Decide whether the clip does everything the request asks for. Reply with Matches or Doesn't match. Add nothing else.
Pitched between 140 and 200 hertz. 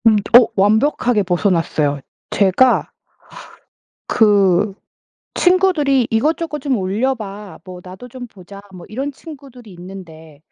Doesn't match